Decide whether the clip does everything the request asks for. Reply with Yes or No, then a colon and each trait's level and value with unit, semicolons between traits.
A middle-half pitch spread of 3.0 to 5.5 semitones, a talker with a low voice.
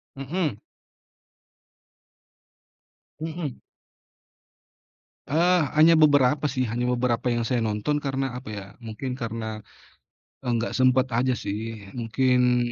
Yes: average, 3.5 semitones; low, 125 Hz